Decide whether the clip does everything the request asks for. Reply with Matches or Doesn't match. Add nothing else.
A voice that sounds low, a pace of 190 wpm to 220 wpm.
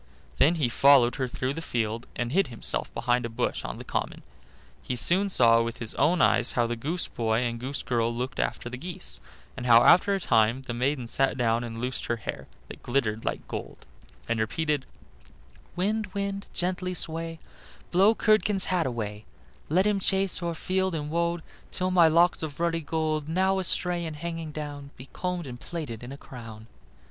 Doesn't match